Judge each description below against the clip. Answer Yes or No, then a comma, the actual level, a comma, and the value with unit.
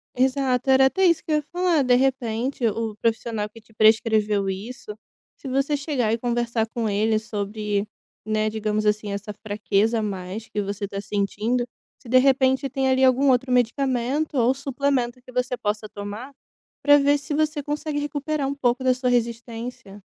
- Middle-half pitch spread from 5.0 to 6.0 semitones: No, average, 4.0 semitones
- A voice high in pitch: Yes, high, 240 Hz